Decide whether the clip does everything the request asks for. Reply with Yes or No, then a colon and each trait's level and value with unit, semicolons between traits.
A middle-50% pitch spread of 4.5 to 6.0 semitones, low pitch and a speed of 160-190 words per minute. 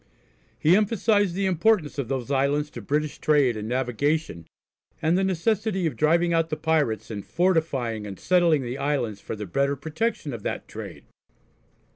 No: wide, 5.4 semitones; medium, 150 Hz; average, 165 wpm